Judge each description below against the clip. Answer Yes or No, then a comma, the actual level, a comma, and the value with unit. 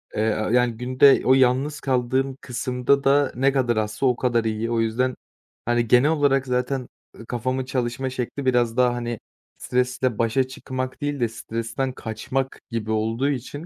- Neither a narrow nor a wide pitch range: No, narrow, 2.1 semitones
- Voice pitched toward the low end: Yes, low, 125 Hz